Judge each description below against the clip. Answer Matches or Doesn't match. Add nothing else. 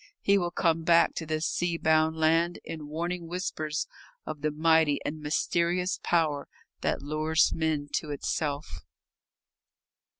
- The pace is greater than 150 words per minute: Doesn't match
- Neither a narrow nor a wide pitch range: Doesn't match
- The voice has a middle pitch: Matches